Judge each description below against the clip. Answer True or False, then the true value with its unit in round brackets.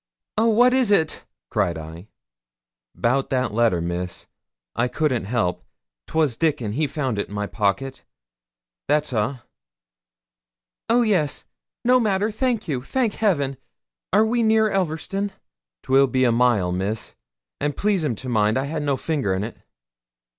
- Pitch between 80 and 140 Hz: True (135 Hz)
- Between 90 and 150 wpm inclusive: True (145 wpm)